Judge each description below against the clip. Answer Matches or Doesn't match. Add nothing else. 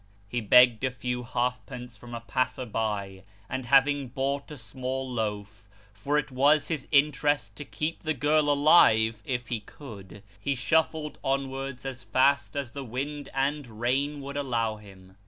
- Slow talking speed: Doesn't match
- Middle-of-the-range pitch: Doesn't match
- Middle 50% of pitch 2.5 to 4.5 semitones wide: Matches